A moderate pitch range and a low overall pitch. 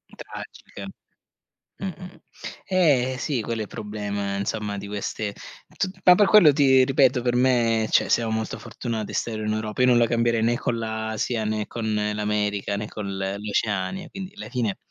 Yes: average, 3.4 semitones; low, 115 Hz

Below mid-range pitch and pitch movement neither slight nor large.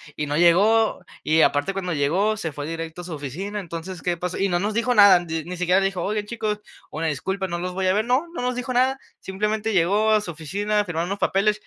No: high, 190 Hz; average, 4.0 semitones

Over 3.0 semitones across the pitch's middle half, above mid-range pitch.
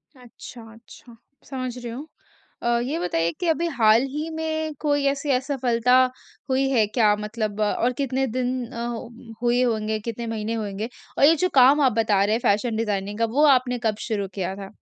Yes: average, 3.6 semitones; high, 240 Hz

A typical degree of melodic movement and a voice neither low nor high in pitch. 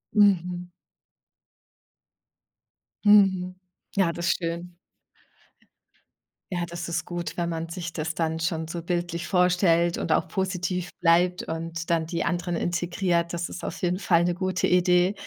No: narrow, 1.2 semitones; medium, 175 Hz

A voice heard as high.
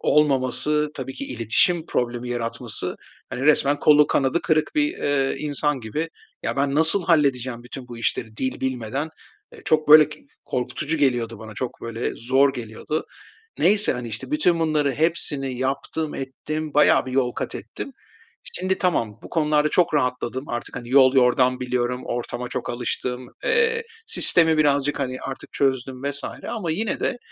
No: low, 135 Hz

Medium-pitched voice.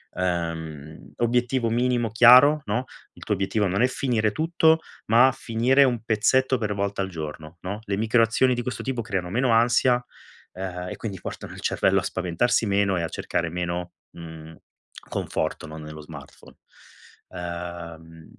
No: low, 100 Hz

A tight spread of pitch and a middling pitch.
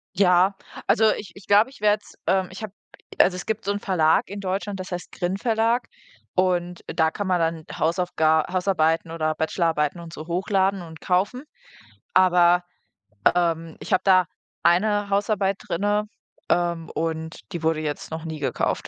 No: average, 3.3 semitones; medium, 180 Hz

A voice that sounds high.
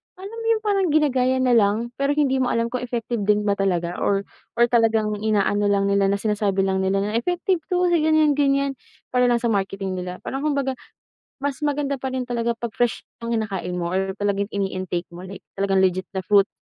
Yes: high, 225 Hz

